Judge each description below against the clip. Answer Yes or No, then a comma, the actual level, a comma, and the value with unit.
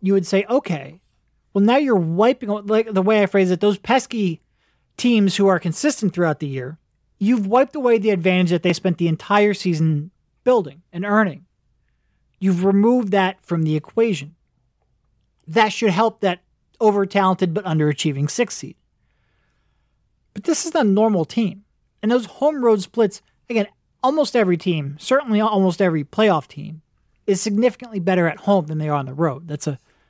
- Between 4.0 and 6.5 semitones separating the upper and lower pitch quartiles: Yes, average, 4.5 semitones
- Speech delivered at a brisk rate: No, average, 175 wpm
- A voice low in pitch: No, high, 195 Hz